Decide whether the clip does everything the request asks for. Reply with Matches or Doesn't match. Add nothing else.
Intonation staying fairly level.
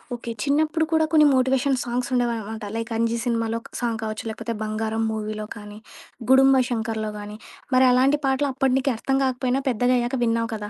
Doesn't match